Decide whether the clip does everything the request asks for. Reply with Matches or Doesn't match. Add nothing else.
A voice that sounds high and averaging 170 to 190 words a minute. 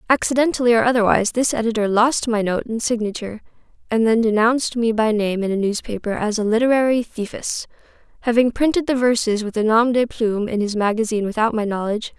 Matches